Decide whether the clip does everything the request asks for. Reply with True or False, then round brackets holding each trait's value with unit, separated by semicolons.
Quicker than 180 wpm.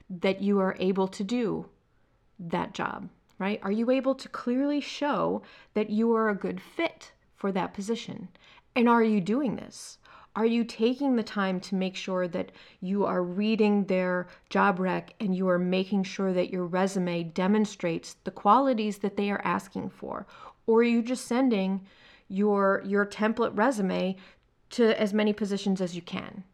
False (170 wpm)